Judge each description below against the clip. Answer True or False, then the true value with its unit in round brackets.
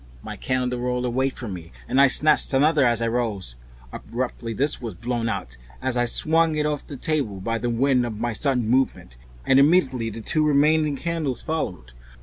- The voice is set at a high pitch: False (125 Hz)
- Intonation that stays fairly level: False (3.9 semitones)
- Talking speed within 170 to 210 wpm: True (190 wpm)